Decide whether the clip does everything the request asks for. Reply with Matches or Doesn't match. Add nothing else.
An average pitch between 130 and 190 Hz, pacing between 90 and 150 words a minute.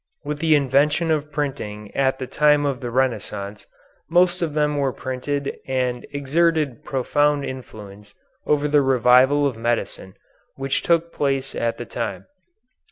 Matches